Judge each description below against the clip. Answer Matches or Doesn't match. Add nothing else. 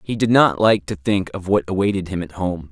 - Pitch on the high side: Doesn't match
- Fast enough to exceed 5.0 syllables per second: Matches